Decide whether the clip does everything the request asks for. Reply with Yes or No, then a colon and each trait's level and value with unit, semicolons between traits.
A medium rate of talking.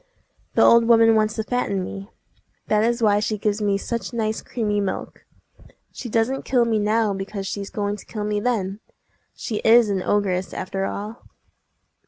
Yes: average, 175 wpm